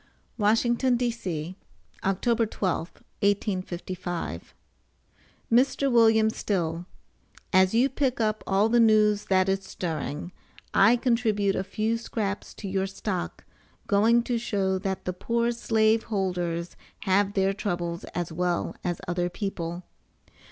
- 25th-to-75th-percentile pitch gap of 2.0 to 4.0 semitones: Yes, average, 3.7 semitones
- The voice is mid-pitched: No, high, 200 Hz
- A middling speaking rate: No, slow, 125 wpm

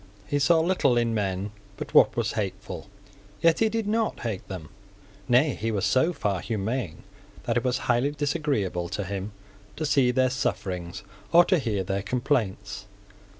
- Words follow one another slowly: No, average, 165 wpm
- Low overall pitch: Yes, low, 120 Hz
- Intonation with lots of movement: Yes, wide, 6.6 semitones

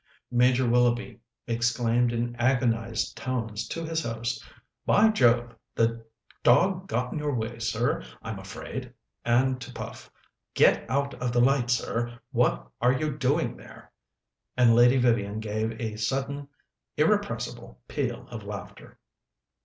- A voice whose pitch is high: No, low, 120 Hz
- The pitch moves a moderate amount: No, narrow, 2.2 semitones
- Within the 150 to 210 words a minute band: No, slow, 135 wpm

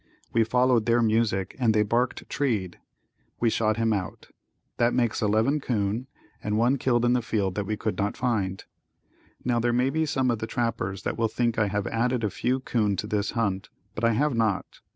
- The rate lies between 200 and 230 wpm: Yes, fast, 205 wpm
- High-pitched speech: No, low, 115 Hz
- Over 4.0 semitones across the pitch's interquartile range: No, narrow, 2.5 semitones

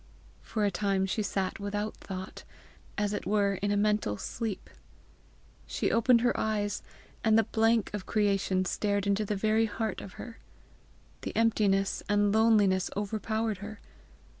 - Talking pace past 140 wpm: Yes, average, 150 wpm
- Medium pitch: No, high, 205 Hz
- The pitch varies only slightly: Yes, narrow, 1.7 semitones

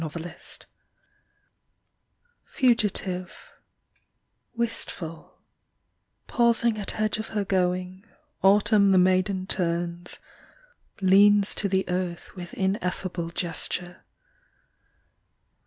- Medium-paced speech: No, slow, 80 wpm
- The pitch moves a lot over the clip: No, narrow, 2.5 semitones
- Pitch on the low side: No, medium, 185 Hz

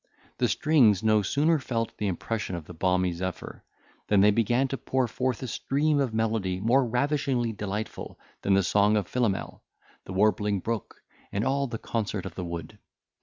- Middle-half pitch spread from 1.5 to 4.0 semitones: No, average, 4.5 semitones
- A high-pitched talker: No, low, 110 Hz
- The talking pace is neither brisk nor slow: Yes, average, 175 wpm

